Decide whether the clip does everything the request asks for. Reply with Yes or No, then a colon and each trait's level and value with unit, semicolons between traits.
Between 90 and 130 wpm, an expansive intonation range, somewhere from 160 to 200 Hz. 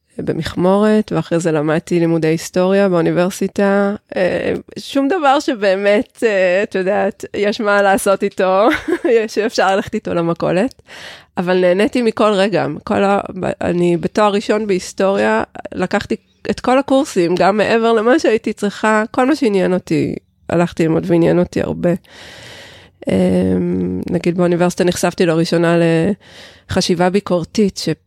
No: average, 120 wpm; average, 3.4 semitones; high, 190 Hz